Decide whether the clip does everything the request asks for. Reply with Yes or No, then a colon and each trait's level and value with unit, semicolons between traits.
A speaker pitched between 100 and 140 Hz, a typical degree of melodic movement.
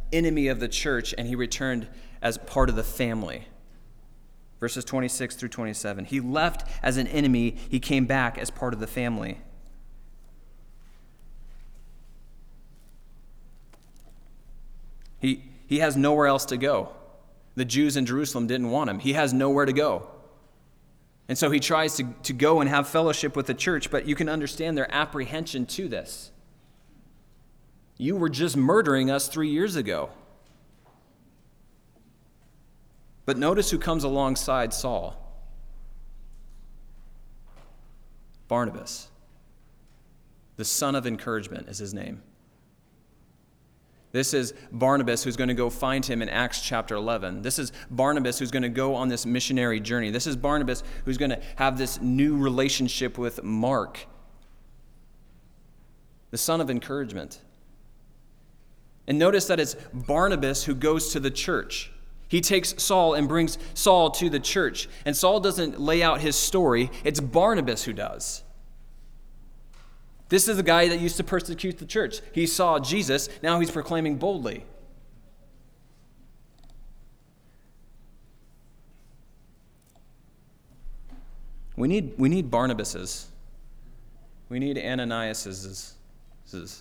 Yes: low, 135 Hz; average, 3.9 semitones